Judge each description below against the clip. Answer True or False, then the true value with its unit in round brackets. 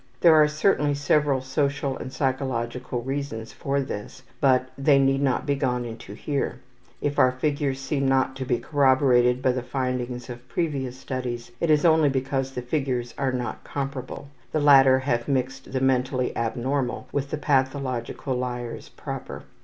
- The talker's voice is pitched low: True (130 Hz)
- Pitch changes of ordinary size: False (1.9 semitones)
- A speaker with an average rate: True (160 wpm)